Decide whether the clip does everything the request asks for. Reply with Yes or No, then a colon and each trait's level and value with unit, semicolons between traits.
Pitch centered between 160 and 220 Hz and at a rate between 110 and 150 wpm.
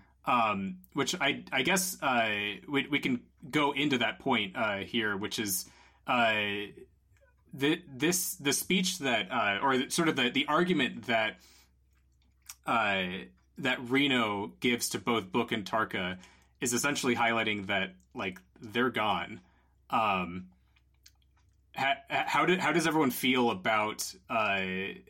No: low, 115 Hz; average, 140 wpm